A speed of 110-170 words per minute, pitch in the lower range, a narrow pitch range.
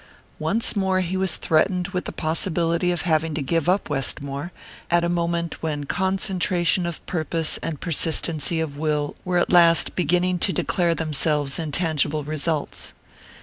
No: average, 155 wpm; medium, 165 Hz; narrow, 2.3 semitones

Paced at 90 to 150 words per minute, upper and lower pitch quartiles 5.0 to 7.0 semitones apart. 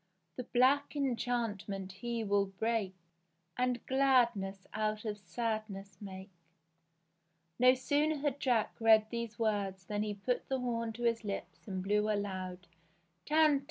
No: average, 140 wpm; average, 3.9 semitones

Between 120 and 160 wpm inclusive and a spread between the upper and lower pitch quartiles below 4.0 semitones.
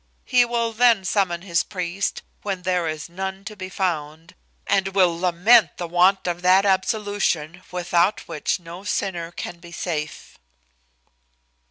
Yes: average, 145 wpm; narrow, 2.5 semitones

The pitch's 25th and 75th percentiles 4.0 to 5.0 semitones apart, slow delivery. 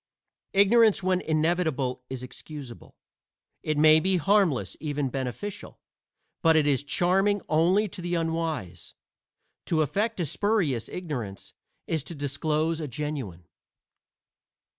Yes: average, 4.4 semitones; slow, 120 wpm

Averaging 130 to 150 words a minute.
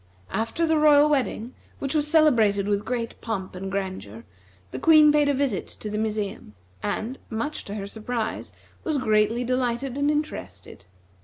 No: average, 160 wpm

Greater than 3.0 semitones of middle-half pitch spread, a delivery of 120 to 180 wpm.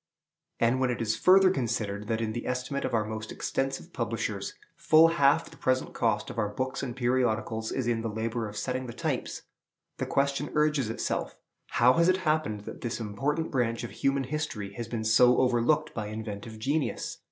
No: average, 3.8 semitones; average, 190 wpm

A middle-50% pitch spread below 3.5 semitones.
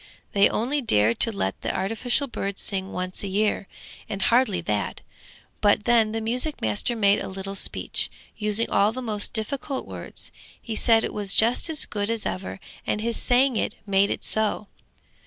Yes: average, 3.0 semitones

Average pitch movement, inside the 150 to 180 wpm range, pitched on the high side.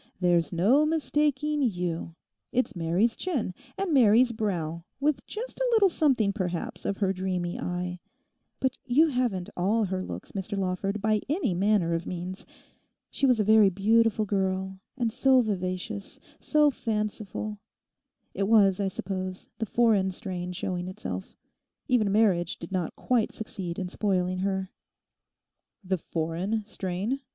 No: average, 4.3 semitones; average, 140 wpm; high, 200 Hz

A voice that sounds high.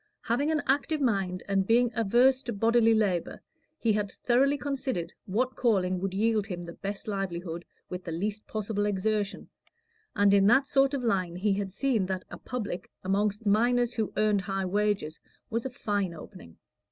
Yes: high, 210 Hz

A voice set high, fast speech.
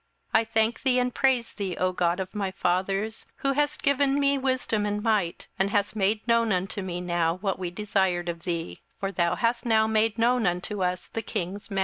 Yes: high, 205 Hz; fast, 220 wpm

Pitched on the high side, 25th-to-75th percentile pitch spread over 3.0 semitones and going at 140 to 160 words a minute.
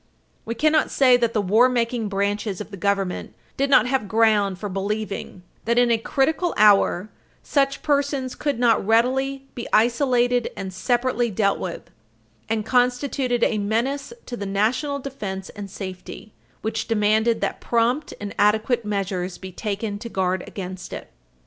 Yes: high, 225 Hz; average, 3.8 semitones; average, 155 wpm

